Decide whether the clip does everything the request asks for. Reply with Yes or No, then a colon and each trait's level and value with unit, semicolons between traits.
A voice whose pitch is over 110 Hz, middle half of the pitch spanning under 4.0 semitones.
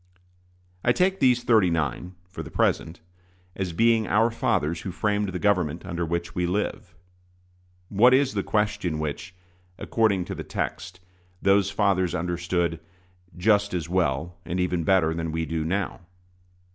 No: very low, 90 Hz; average, 3.4 semitones